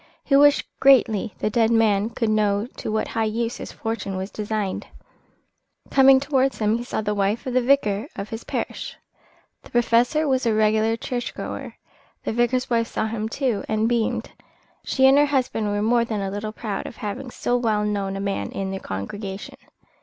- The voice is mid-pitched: No, high, 225 Hz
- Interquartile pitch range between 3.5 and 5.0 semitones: No, average, 2.8 semitones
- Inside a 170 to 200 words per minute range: Yes, average, 190 wpm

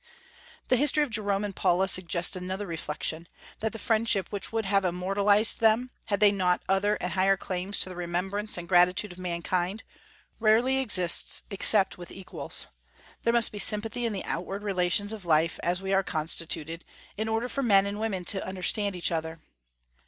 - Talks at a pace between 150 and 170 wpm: No, average, 180 wpm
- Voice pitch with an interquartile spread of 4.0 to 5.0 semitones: No, average, 3.0 semitones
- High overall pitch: Yes, high, 195 Hz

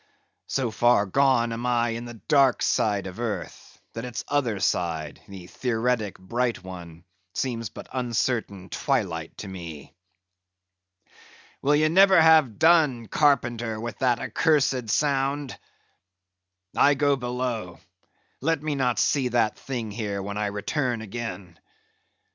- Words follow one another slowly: Yes, slow, 130 wpm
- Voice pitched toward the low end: Yes, low, 120 Hz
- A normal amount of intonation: Yes, average, 4.8 semitones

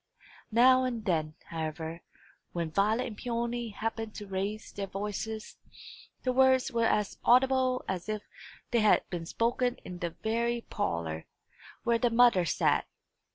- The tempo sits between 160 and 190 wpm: No, average, 145 wpm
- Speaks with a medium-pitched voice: No, high, 220 Hz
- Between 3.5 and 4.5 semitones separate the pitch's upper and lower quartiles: Yes, average, 4.1 semitones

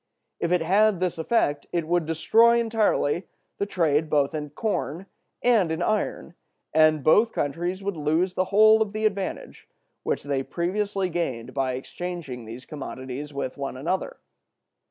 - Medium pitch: Yes, medium, 170 Hz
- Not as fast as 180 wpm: Yes, average, 155 wpm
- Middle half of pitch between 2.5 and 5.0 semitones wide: No, wide, 5.5 semitones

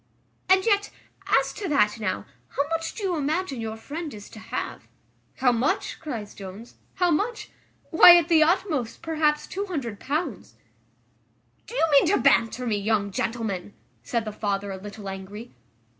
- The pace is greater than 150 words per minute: Yes, average, 160 wpm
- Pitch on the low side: No, very high, 265 Hz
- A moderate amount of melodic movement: No, wide, 7.8 semitones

